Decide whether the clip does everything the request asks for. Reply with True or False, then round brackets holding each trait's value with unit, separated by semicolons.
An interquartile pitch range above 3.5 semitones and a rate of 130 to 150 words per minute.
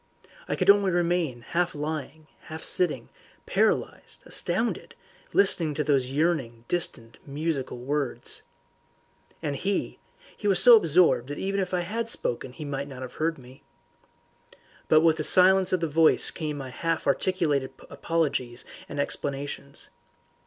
True (4.3 semitones; 145 wpm)